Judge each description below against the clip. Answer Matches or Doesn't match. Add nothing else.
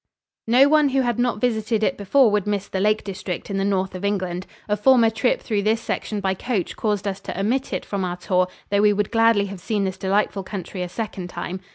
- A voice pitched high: Matches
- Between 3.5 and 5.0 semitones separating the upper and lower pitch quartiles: Doesn't match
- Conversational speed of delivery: Doesn't match